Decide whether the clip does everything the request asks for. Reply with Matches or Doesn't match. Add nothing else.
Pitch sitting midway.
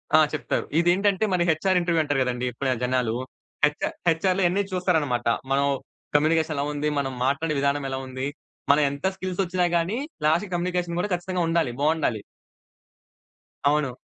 Matches